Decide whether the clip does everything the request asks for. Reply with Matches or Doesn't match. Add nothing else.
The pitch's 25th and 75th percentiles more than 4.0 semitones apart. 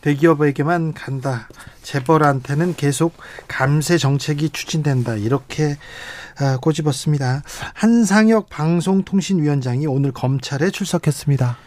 Doesn't match